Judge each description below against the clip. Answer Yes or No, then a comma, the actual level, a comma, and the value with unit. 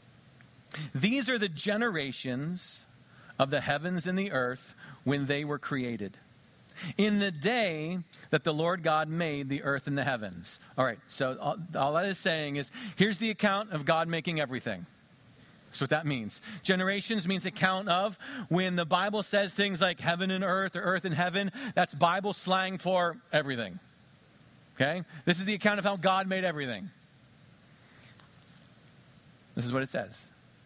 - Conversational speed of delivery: Yes, average, 160 wpm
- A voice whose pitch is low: No, medium, 165 Hz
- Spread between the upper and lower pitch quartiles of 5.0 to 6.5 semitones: Yes, average, 5.3 semitones